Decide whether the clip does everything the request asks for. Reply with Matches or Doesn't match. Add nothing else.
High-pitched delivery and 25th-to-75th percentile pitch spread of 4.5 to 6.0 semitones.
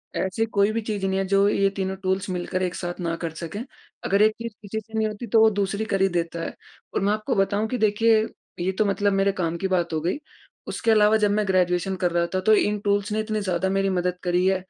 Doesn't match